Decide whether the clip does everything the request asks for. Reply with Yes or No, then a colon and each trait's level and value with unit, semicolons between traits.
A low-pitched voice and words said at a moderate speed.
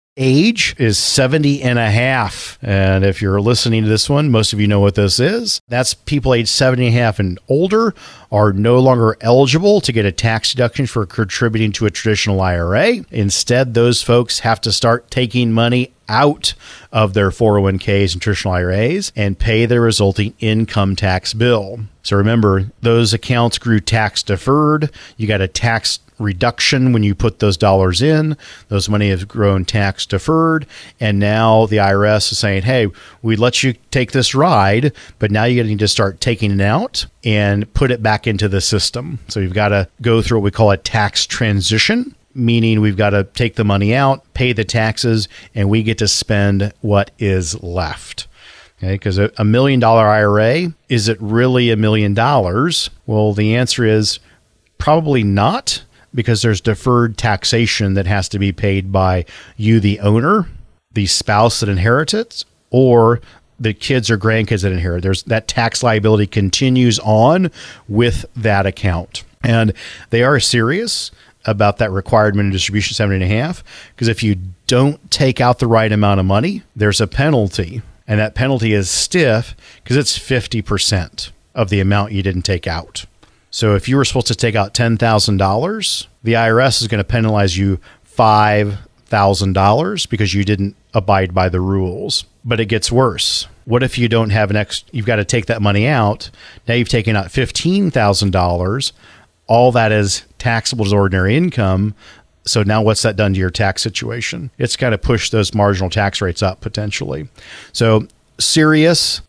Yes: low, 110 Hz; average, 175 wpm